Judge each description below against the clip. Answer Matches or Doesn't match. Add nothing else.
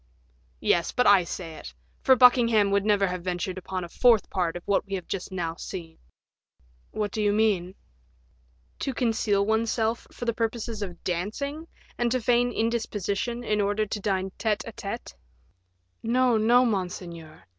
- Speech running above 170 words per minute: Doesn't match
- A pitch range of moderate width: Matches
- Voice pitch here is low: Doesn't match